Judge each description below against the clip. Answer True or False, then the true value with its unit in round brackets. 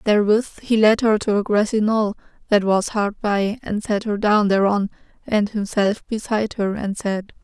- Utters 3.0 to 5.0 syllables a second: True (4.7 syllables/s)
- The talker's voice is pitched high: True (210 Hz)